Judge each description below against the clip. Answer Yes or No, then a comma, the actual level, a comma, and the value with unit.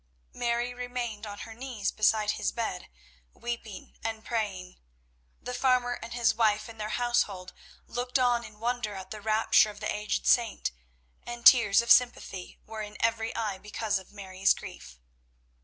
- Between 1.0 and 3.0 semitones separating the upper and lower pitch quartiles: Yes, narrow, 2.4 semitones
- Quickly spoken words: No, average, 160 wpm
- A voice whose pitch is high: Yes, high, 225 Hz